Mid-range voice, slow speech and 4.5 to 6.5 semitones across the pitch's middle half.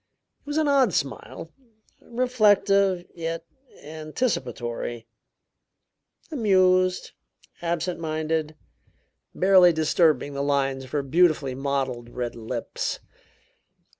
Yes: medium, 160 Hz; slow, 90 wpm; average, 5.2 semitones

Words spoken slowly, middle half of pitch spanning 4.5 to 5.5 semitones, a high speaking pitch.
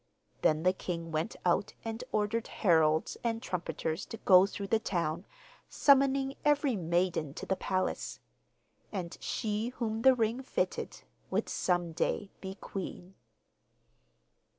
Yes: slow, 130 wpm; average, 4.8 semitones; high, 195 Hz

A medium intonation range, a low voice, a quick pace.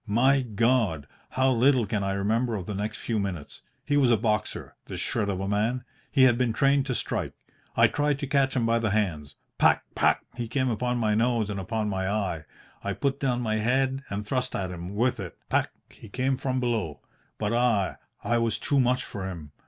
Yes: average, 4.1 semitones; low, 115 Hz; fast, 215 wpm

